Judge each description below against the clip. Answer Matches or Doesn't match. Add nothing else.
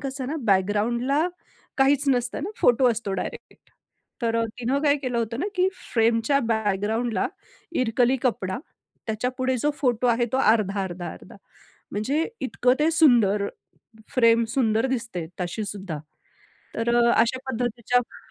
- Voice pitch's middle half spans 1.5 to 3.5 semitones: Matches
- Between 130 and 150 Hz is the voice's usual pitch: Doesn't match